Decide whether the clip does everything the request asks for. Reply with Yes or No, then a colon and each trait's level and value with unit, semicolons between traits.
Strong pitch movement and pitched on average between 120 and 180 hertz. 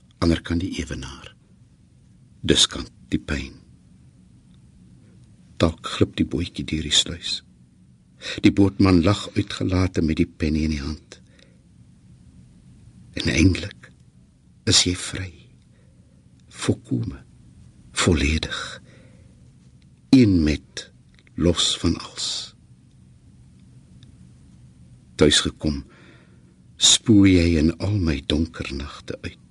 No: wide, 6.4 semitones; very low, 75 Hz